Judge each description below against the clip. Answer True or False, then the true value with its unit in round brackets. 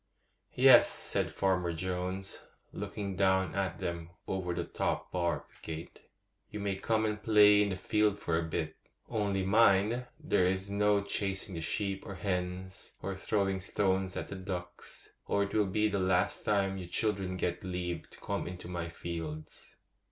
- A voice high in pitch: False (95 Hz)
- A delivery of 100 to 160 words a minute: False (180 wpm)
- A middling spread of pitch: False (2.1 semitones)